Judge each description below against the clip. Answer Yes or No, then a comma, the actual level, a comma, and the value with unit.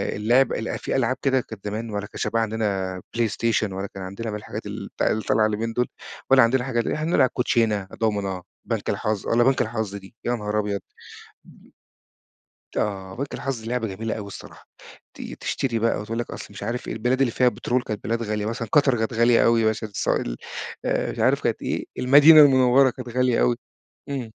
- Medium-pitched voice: No, low, 115 Hz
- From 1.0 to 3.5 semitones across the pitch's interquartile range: Yes, average, 2.9 semitones